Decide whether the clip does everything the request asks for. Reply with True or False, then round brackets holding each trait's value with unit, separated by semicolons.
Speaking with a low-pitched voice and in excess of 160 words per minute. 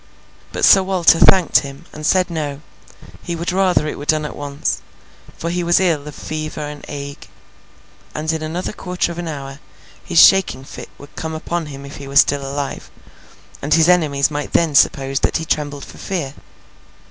False (155 Hz; 190 wpm)